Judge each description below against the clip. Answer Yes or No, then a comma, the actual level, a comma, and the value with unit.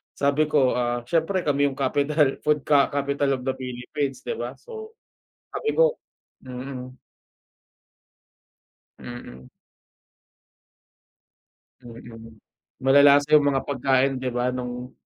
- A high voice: No, low, 135 Hz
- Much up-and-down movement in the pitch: No, average, 2.7 semitones